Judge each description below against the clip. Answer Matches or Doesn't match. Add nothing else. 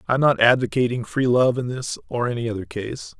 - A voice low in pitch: Matches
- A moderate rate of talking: Doesn't match